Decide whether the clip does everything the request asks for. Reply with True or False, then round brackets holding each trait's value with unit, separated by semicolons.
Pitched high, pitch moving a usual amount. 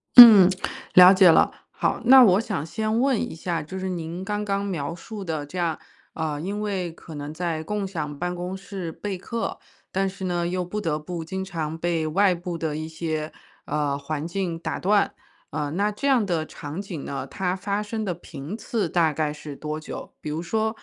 False (175 Hz; 4.0 semitones)